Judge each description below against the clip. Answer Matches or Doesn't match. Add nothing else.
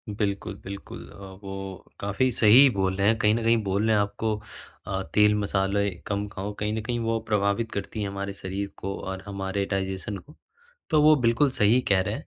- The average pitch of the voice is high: Doesn't match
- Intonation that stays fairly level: Matches